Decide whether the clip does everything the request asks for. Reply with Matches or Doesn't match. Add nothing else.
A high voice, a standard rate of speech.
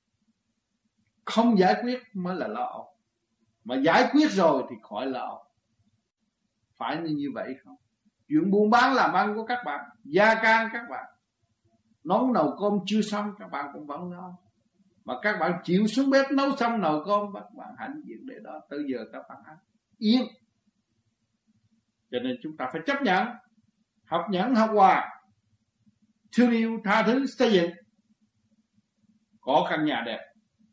Doesn't match